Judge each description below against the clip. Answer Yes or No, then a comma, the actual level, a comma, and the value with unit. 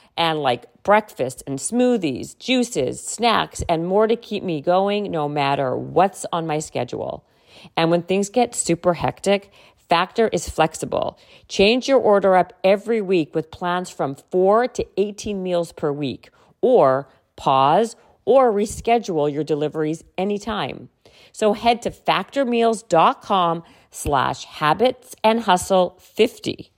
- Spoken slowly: Yes, slow, 130 wpm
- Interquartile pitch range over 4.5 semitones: Yes, wide, 5.4 semitones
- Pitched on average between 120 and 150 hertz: No, medium, 185 Hz